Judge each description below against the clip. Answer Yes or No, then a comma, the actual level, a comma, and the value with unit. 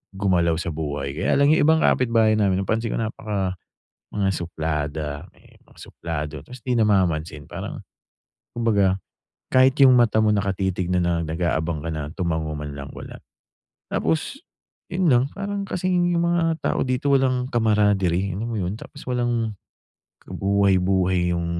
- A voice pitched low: Yes, low, 100 Hz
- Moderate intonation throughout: No, wide, 6.0 semitones